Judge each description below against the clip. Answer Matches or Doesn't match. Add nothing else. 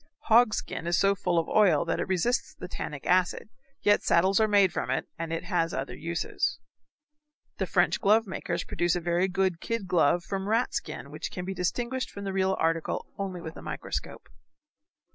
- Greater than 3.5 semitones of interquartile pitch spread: Doesn't match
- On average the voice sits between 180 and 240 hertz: Matches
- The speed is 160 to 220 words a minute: Matches